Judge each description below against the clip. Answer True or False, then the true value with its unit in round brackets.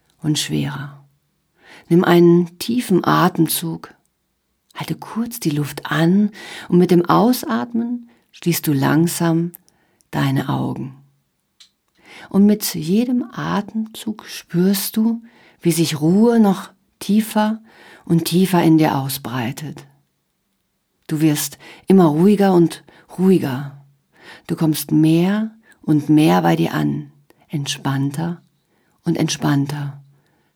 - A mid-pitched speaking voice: True (165 Hz)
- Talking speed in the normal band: False (105 wpm)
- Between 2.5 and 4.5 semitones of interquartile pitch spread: False (5.2 semitones)